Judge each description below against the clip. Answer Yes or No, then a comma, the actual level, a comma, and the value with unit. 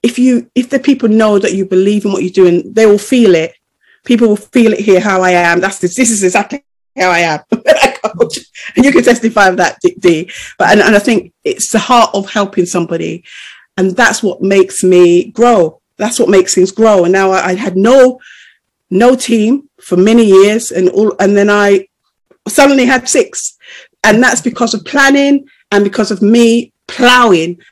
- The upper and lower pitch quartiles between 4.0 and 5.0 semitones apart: Yes, average, 4.6 semitones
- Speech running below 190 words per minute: No, average, 195 wpm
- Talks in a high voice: Yes, high, 215 Hz